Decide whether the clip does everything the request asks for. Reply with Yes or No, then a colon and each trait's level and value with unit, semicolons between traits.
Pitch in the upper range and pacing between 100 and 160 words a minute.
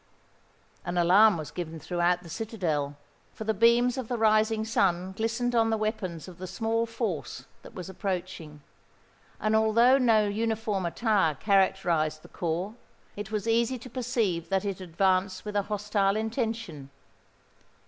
Yes: high, 205 Hz; average, 150 wpm